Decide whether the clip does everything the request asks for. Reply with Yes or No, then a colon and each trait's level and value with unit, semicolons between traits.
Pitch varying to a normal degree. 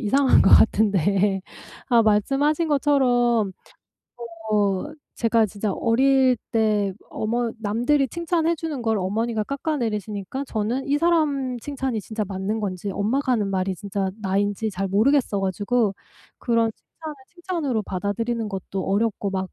Yes: average, 4.9 semitones